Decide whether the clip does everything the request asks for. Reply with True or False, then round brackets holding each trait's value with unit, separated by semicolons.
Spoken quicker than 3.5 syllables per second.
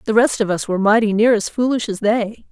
True (6.0 syllables/s)